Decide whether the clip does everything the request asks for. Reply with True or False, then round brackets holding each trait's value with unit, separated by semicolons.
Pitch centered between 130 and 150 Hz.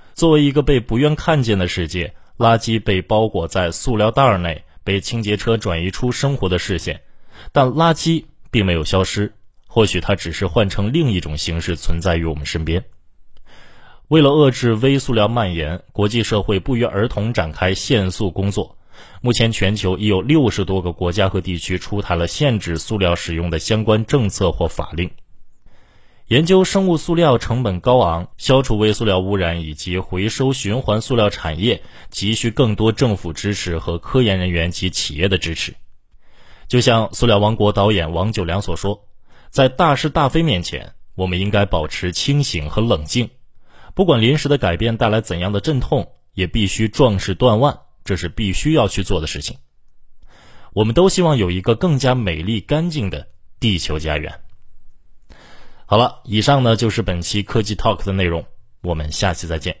False (105 Hz)